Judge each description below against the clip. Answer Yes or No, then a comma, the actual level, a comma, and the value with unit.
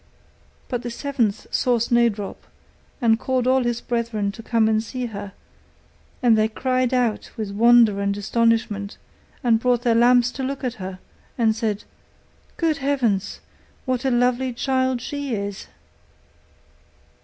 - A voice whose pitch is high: Yes, high, 235 Hz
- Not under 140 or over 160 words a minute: Yes, average, 145 wpm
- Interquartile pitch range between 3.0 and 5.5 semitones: No, narrow, 2.6 semitones